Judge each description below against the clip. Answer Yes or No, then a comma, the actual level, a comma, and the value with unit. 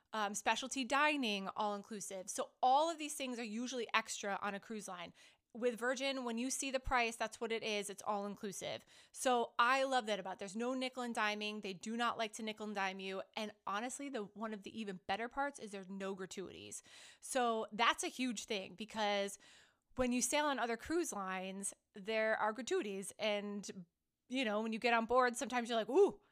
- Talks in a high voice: Yes, high, 225 Hz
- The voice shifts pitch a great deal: No, average, 3.8 semitones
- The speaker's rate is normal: No, fast, 210 wpm